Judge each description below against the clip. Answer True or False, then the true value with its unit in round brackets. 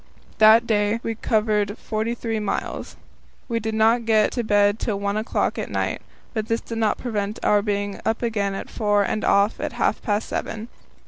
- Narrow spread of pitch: True (1.7 semitones)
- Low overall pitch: False (215 Hz)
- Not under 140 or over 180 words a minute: False (190 wpm)